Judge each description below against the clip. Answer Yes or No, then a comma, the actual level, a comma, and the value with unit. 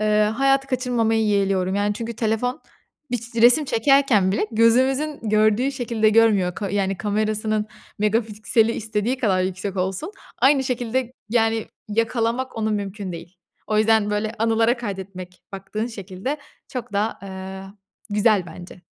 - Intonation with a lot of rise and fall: No, average, 2.9 semitones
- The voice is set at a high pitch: Yes, high, 220 Hz